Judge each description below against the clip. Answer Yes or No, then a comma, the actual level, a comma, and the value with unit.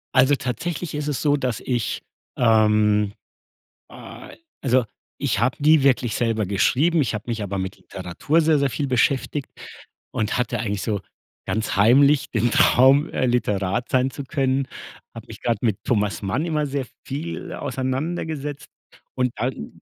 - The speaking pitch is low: Yes, low, 125 Hz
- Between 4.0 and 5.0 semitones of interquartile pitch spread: Yes, average, 4.7 semitones